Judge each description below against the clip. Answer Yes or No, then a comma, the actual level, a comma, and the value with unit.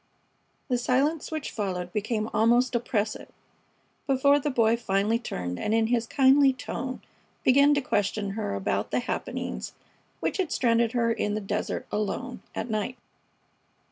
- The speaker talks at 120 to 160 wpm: Yes, average, 145 wpm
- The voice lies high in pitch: Yes, high, 230 Hz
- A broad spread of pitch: No, average, 3.6 semitones